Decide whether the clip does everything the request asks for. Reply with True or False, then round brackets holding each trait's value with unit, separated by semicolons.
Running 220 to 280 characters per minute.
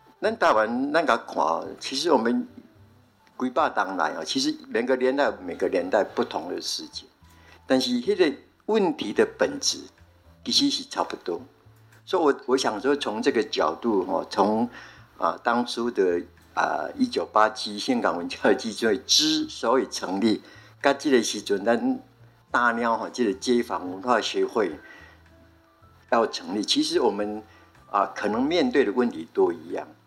True (225 characters per minute)